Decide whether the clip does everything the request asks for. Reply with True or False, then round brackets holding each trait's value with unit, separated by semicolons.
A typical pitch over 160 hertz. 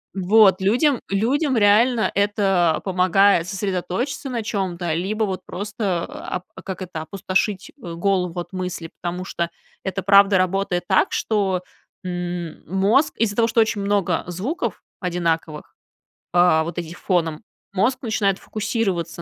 True (190 Hz)